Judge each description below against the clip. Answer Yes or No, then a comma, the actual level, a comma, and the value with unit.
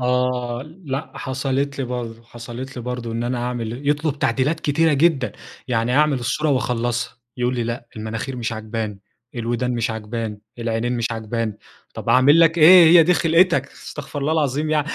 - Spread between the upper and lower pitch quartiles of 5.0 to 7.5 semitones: No, average, 3.6 semitones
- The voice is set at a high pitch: No, low, 125 Hz